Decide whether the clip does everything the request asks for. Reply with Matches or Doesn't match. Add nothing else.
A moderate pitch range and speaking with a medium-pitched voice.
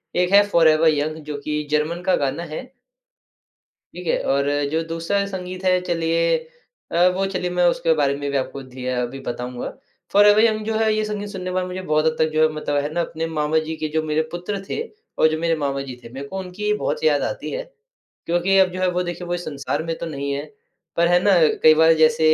Matches